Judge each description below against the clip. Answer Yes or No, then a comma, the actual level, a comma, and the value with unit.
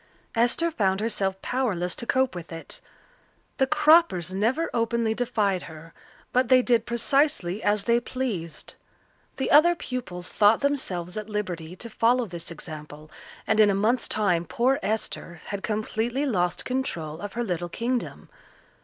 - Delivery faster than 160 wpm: No, average, 150 wpm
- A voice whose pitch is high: Yes, high, 215 Hz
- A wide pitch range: Yes, wide, 5.9 semitones